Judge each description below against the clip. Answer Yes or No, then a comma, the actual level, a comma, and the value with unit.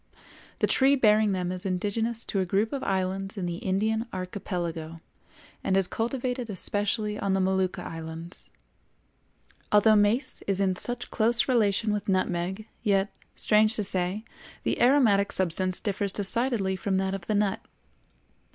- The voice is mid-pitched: No, high, 200 Hz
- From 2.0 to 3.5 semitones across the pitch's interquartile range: Yes, average, 2.7 semitones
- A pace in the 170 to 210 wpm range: No, average, 150 wpm